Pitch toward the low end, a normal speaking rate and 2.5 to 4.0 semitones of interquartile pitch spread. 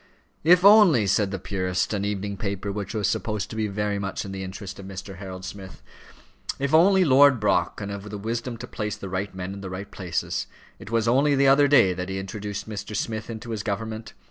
No: low, 105 Hz; fast, 220 wpm; average, 3.1 semitones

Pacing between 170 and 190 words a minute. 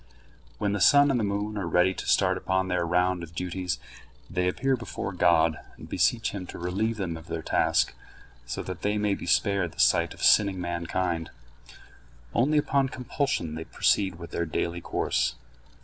Yes: average, 180 wpm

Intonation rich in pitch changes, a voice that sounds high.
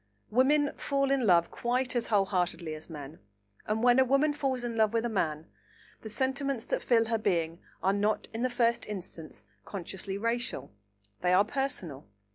Yes: wide, 6.0 semitones; high, 220 Hz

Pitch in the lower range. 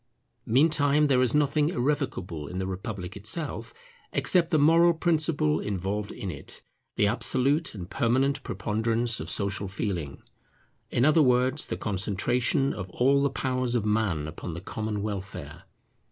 Yes: low, 115 Hz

